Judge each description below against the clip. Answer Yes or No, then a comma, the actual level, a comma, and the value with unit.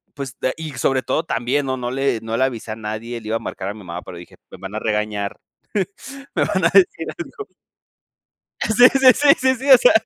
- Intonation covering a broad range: Yes, wide, 7.2 semitones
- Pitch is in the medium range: No, low, 125 Hz